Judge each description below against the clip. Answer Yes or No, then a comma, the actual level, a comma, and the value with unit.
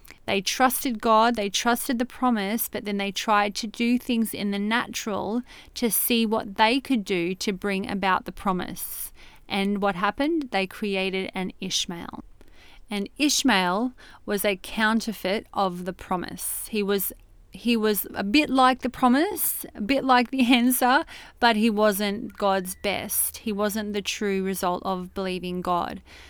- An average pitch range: Yes, average, 3.9 semitones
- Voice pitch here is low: No, high, 210 Hz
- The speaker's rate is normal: Yes, average, 160 wpm